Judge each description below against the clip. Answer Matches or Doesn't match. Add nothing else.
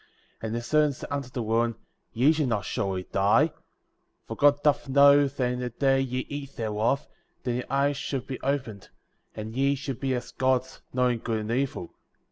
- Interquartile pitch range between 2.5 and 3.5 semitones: Matches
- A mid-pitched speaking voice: Doesn't match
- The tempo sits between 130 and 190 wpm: Doesn't match